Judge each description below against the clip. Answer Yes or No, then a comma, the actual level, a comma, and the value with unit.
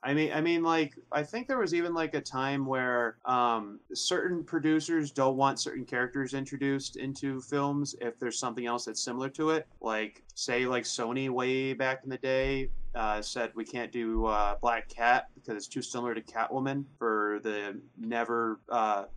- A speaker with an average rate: Yes, average, 185 wpm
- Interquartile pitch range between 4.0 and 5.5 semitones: No, average, 3.0 semitones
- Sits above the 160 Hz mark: No, low, 130 Hz